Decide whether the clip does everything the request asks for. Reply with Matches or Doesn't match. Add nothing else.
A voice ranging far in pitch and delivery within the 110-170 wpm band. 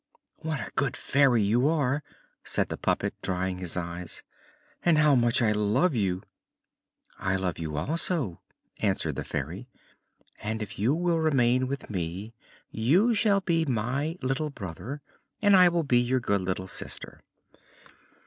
Matches